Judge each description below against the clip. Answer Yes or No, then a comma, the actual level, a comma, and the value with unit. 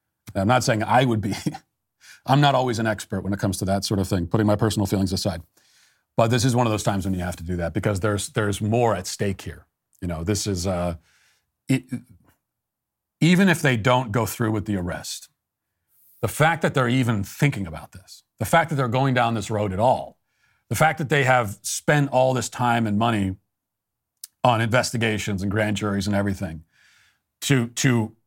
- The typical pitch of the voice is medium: No, low, 110 Hz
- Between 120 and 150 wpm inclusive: No, fast, 205 wpm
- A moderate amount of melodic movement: Yes, average, 4.0 semitones